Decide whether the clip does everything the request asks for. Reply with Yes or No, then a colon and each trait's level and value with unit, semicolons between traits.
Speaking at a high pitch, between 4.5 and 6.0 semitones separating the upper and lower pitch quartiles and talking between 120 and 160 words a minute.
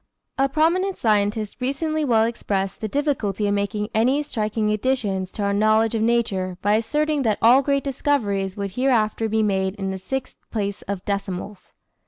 No: high, 215 Hz; average, 4.8 semitones; average, 170 wpm